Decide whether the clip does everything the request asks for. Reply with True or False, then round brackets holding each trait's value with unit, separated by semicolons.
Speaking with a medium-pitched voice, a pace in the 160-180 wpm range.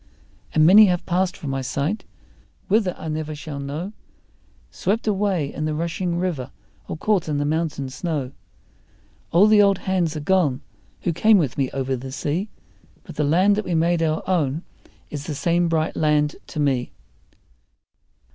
True (160 Hz; 170 wpm)